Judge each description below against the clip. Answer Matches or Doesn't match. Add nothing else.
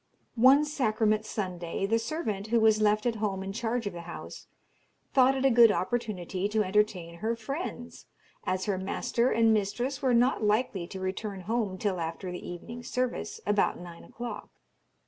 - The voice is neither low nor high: Doesn't match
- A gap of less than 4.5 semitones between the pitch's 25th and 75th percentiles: Matches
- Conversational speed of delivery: Matches